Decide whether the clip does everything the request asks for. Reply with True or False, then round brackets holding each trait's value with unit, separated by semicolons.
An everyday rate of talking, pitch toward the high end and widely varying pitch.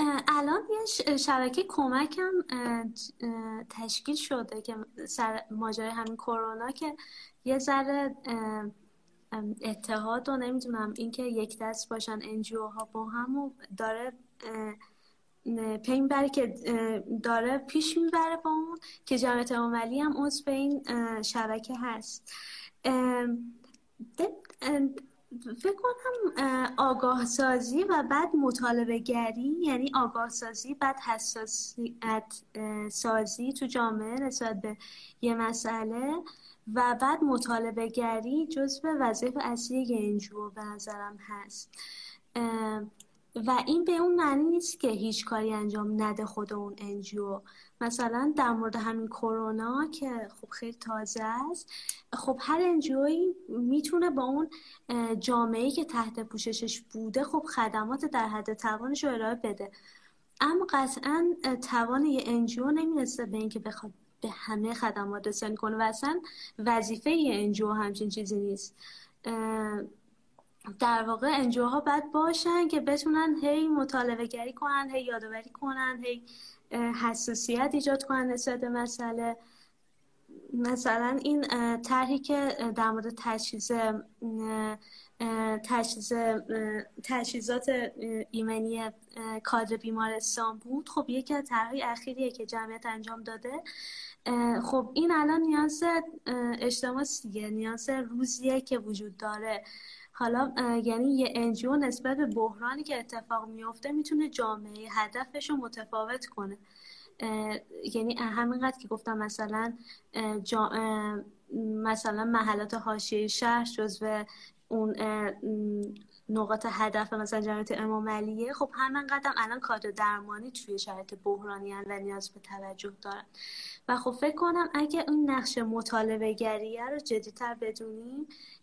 False (120 wpm; 235 Hz; 3.5 semitones)